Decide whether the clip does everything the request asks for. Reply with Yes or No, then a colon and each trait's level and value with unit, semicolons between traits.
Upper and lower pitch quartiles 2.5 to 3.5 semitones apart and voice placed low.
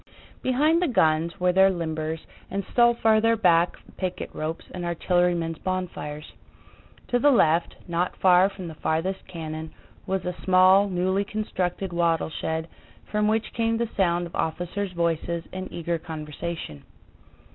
No: average, 3.0 semitones; medium, 180 Hz